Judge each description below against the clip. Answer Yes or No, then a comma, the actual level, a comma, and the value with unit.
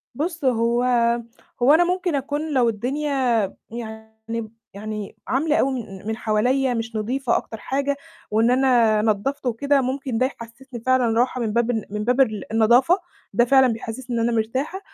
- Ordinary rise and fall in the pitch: Yes, average, 3.3 semitones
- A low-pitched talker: No, high, 245 Hz